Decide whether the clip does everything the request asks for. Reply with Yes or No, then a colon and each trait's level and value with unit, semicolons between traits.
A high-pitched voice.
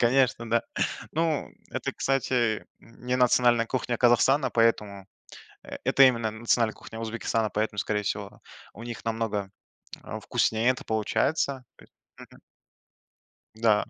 No: low, 115 Hz